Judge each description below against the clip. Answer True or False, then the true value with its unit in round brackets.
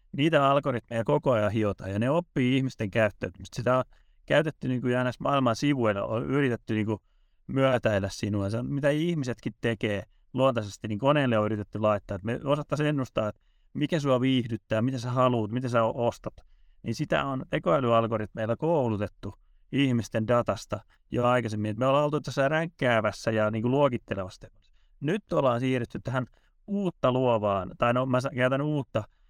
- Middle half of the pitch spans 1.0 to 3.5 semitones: False (4.0 semitones)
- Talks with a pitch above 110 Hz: True (120 Hz)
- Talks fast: True (160 wpm)